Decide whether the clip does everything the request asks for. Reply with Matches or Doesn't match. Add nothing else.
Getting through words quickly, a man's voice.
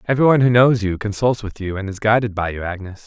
Matches